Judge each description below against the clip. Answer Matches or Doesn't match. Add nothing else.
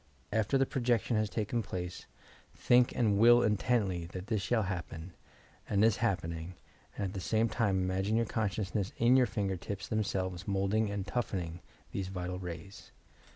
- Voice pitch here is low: Matches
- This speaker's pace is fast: Doesn't match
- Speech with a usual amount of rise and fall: Matches